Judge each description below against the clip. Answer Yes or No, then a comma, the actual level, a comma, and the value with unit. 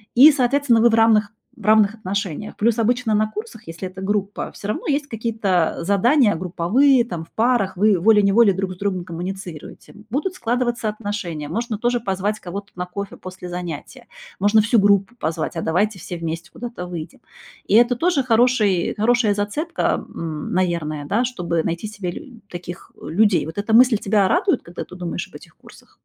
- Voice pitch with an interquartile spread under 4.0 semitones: No, average, 4.6 semitones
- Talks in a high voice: Yes, high, 205 Hz